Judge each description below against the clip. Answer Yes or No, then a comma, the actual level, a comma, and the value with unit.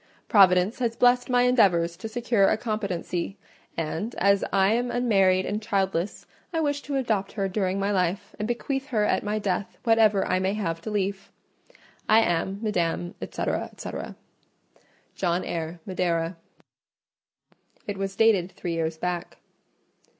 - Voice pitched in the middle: No, high, 195 Hz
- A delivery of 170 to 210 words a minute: No, average, 150 wpm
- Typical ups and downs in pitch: Yes, average, 3.6 semitones